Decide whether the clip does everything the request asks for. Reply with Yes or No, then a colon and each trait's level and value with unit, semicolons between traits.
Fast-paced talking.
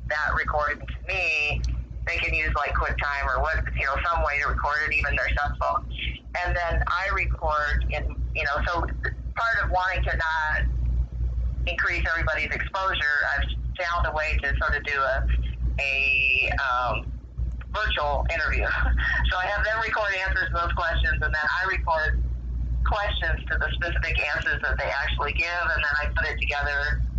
No: average, 175 wpm